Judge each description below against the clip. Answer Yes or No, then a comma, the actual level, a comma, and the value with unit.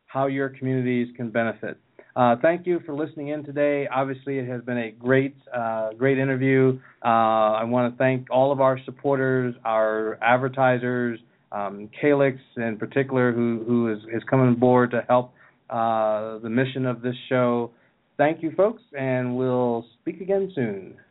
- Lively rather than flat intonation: No, narrow, 2.5 semitones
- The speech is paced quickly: No, average, 160 wpm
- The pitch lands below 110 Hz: No, low, 125 Hz